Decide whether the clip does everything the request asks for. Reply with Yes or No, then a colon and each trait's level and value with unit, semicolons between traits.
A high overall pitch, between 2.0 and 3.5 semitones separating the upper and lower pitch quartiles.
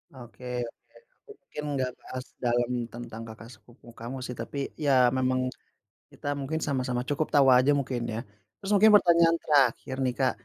No: low, 130 Hz; average, 2.8 semitones